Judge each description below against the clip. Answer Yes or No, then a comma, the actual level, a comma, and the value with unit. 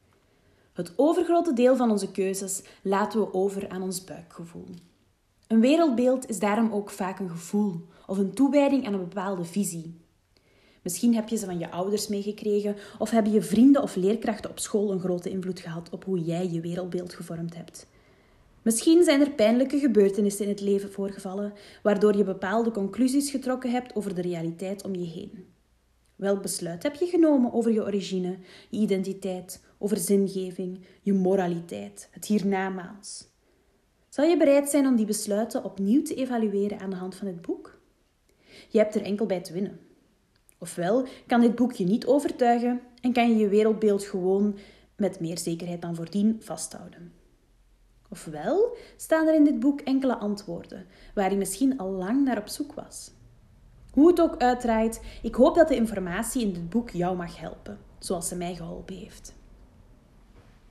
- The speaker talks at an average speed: Yes, average, 170 wpm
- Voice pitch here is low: No, high, 200 Hz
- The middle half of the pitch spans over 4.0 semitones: Yes, average, 4.4 semitones